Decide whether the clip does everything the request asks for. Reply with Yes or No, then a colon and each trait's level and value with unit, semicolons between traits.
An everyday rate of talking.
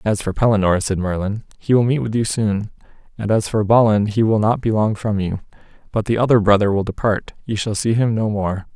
No: fast, 235 wpm